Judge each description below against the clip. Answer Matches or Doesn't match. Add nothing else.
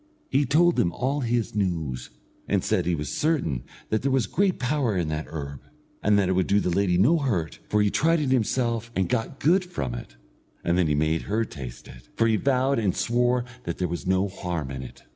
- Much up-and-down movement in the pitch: Matches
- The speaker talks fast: Matches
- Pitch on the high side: Doesn't match